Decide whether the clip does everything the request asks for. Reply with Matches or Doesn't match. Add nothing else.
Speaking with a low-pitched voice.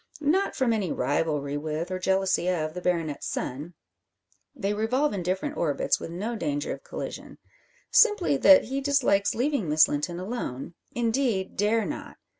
Doesn't match